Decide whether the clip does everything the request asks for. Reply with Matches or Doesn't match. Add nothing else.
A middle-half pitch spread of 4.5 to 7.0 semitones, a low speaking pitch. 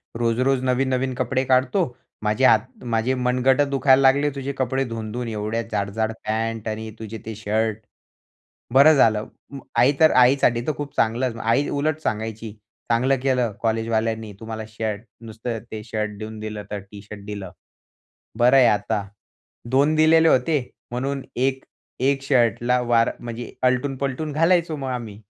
Doesn't match